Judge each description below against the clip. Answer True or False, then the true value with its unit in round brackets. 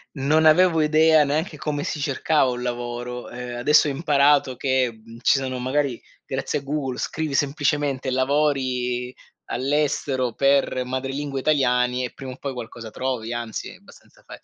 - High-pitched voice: False (135 Hz)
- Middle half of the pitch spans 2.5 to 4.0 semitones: True (2.9 semitones)